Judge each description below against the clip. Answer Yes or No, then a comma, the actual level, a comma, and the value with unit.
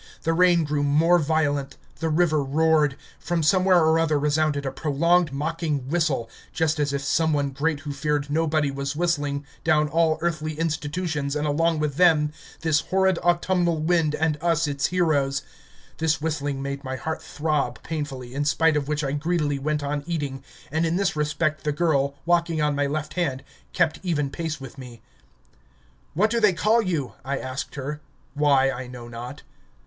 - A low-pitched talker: No, medium, 150 Hz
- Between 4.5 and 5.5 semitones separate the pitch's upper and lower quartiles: No, narrow, 2.5 semitones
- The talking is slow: No, average, 175 wpm